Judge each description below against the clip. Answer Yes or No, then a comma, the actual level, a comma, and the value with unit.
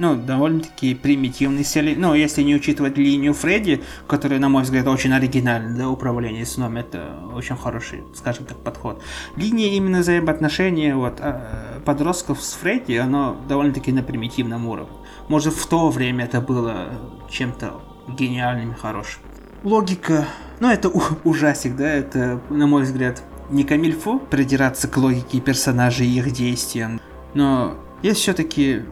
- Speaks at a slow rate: No, average, 145 wpm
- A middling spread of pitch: Yes, average, 3.3 semitones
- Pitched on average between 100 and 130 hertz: No, medium, 140 Hz